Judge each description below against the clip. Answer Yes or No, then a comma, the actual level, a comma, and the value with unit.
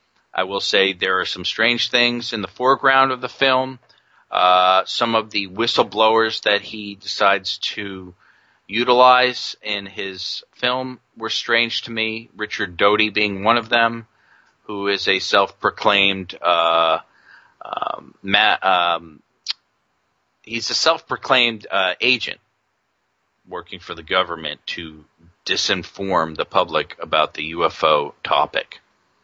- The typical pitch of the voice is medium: No, low, 110 Hz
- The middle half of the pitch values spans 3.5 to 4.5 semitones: Yes, average, 3.8 semitones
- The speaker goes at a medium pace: No, slow, 125 wpm